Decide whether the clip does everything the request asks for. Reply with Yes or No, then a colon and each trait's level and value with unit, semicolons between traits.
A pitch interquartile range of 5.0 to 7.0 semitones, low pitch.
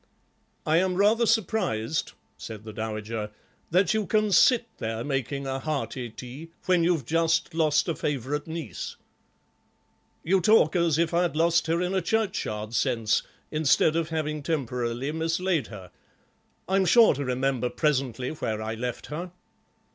No: wide, 5.5 semitones; medium, 155 Hz